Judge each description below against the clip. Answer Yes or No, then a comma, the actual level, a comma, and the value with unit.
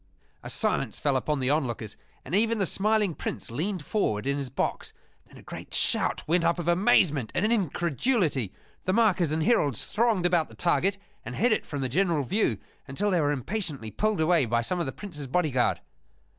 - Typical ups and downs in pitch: No, wide, 6.4 semitones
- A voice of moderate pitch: Yes, medium, 170 Hz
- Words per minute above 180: Yes, average, 195 wpm